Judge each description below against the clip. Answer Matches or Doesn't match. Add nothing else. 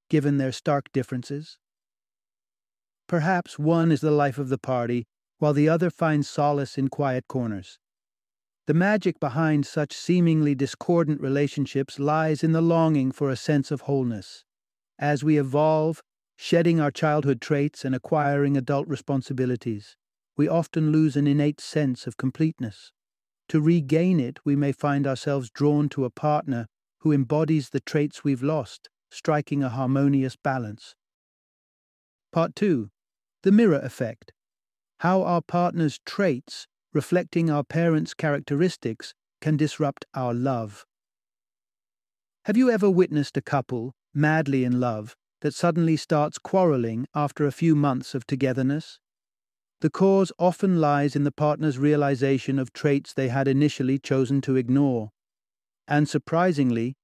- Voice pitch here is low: Doesn't match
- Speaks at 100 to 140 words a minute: Matches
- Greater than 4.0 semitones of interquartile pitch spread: Doesn't match